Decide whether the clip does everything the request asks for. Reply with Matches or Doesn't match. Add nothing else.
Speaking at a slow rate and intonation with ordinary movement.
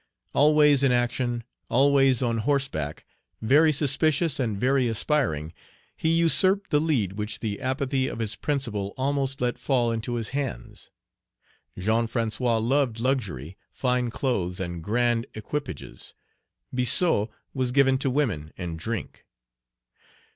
Matches